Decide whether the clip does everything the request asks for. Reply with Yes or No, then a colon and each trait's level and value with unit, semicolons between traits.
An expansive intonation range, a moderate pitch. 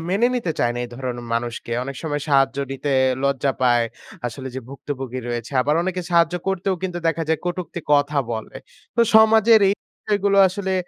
Yes: wide, 6.3 semitones; medium, 145 Hz